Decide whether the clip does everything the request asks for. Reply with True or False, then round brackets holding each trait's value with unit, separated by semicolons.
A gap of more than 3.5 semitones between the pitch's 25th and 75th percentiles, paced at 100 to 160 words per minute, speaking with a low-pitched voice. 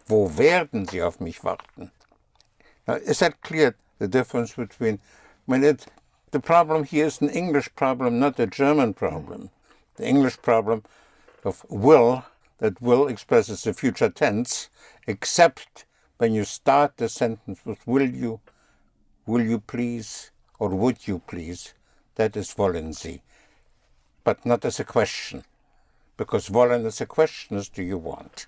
True (4.6 semitones; 150 wpm; 115 Hz)